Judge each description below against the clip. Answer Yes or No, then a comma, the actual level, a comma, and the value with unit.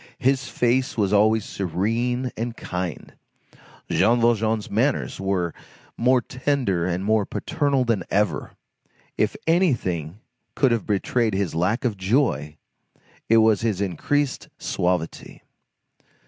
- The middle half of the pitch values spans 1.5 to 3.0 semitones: No, average, 4.7 semitones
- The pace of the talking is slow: Yes, slow, 120 wpm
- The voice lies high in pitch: No, low, 110 Hz